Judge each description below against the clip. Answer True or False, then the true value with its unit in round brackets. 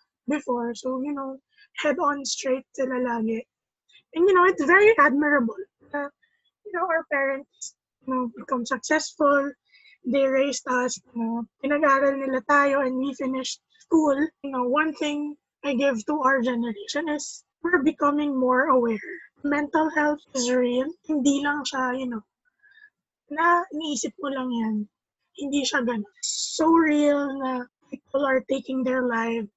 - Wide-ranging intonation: False (2.9 semitones)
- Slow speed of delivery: False (150 wpm)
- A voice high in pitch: True (280 Hz)